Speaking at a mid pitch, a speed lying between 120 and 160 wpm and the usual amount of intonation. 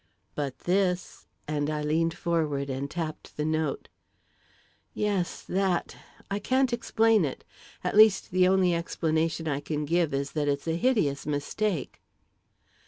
Yes: medium, 165 Hz; average, 140 wpm; average, 4.3 semitones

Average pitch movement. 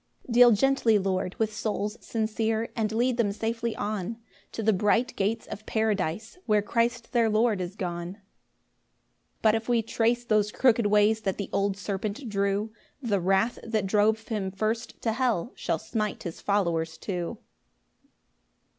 No: narrow, 2.3 semitones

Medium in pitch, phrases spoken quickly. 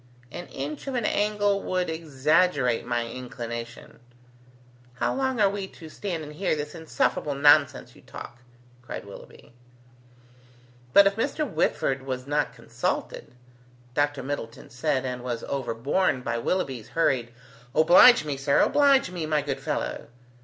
No: medium, 145 Hz; average, 145 wpm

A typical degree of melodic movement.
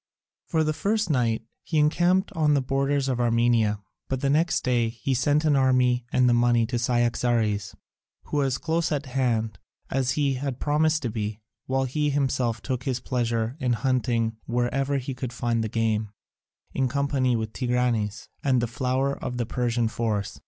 Yes: average, 3.0 semitones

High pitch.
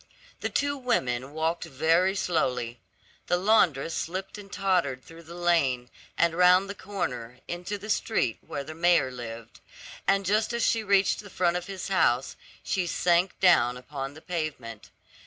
No: medium, 170 Hz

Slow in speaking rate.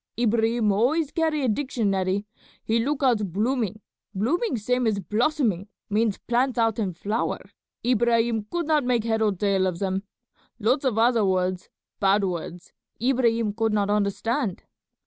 No: average, 145 wpm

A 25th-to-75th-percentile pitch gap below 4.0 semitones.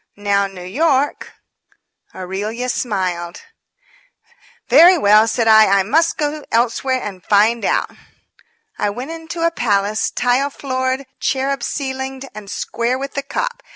No: average, 5.2 semitones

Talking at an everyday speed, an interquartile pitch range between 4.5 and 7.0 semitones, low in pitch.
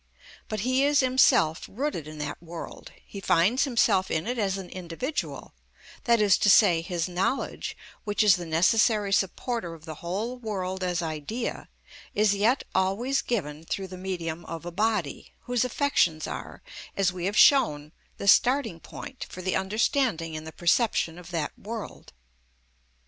No: average, 160 wpm; average, 5.3 semitones; high, 190 Hz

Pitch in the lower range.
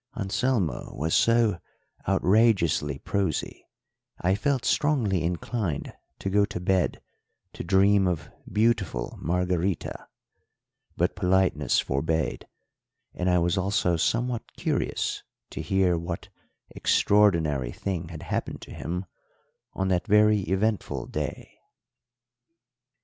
Yes: very low, 95 Hz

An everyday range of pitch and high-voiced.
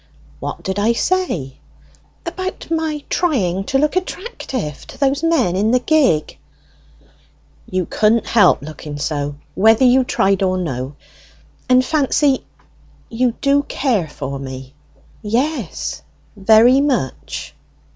No: wide, 8.4 semitones; high, 230 Hz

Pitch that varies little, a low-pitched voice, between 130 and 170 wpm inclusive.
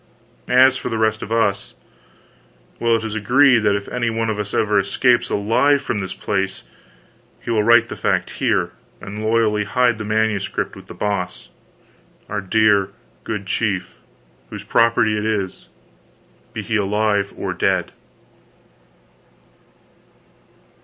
Yes: narrow, 2.2 semitones; low, 110 Hz; average, 140 wpm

